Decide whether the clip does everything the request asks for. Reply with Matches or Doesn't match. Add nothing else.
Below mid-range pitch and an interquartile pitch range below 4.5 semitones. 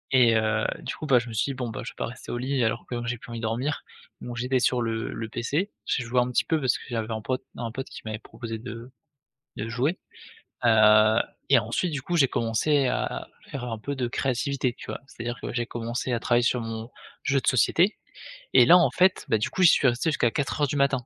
Matches